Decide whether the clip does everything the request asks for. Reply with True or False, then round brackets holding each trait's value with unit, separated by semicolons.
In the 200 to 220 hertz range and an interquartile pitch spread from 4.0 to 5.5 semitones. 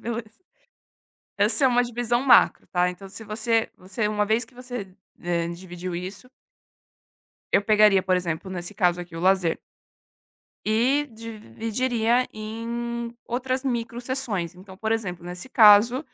True (215 Hz; 4.3 semitones)